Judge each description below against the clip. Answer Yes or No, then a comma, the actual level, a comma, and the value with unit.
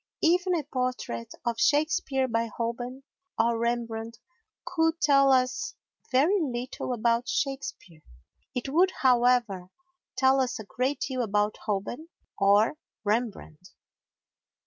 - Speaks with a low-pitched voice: No, high, 245 Hz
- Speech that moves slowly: Yes, slow, 115 wpm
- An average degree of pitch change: Yes, average, 3.4 semitones